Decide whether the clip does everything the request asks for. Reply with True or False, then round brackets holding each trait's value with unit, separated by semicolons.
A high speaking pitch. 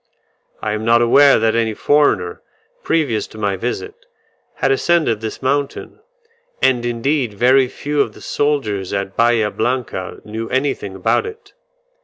False (120 Hz)